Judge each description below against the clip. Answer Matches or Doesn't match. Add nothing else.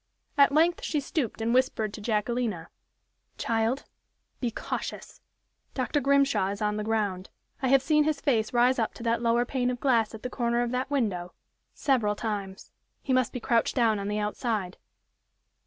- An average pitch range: Matches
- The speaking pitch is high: Matches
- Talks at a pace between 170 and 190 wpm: Matches